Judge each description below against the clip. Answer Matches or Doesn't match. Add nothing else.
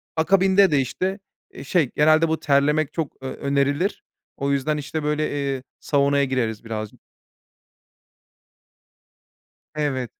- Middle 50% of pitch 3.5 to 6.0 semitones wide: Doesn't match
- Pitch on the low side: Doesn't match